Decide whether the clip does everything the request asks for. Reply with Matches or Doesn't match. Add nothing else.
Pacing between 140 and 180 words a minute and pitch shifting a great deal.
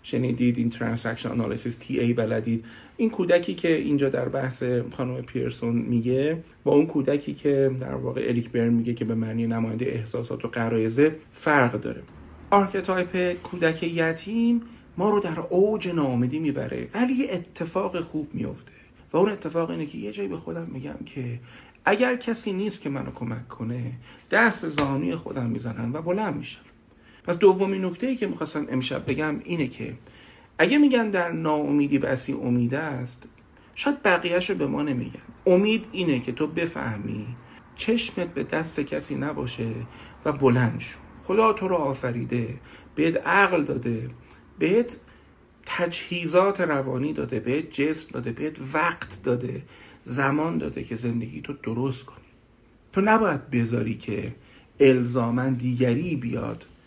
Matches